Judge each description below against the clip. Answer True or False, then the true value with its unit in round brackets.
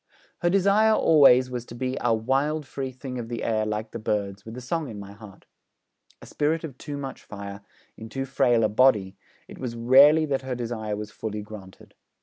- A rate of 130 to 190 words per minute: False (205 wpm)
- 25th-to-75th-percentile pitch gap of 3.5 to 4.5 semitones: True (4.2 semitones)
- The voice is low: True (120 Hz)